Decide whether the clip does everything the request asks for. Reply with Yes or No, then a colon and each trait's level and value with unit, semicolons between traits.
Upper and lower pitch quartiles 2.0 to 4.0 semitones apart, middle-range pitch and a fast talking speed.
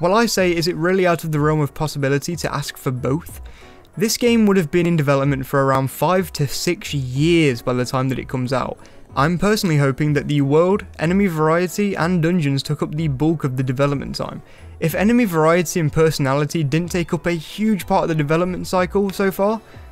No: average, 4.4 semitones; medium, 160 Hz; fast, 215 wpm